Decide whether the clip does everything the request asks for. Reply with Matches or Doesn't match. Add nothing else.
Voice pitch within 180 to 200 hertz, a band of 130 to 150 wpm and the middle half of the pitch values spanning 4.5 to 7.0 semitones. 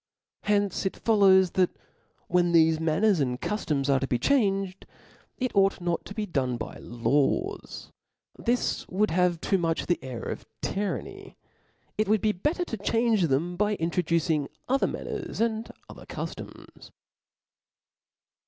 Matches